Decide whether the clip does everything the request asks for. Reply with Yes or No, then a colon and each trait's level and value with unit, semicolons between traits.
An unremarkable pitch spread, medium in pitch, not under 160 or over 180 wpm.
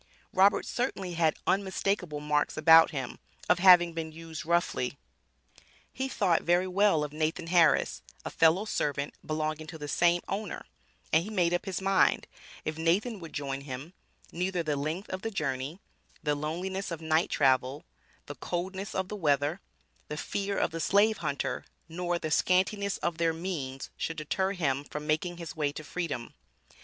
Yes: average, 3.6 semitones; medium, 165 Hz; average, 170 wpm